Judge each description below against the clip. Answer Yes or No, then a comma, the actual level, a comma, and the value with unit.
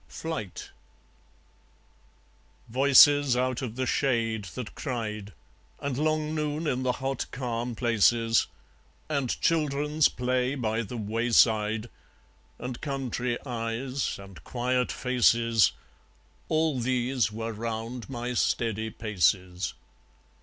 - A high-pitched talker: No, low, 125 Hz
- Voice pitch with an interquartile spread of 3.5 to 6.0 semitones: No, average, 3.0 semitones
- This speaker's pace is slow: Yes, slow, 105 wpm